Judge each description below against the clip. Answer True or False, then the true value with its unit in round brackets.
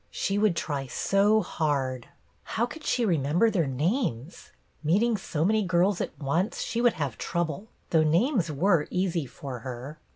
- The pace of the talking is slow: False (160 wpm)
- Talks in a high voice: False (170 Hz)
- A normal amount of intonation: False (6.3 semitones)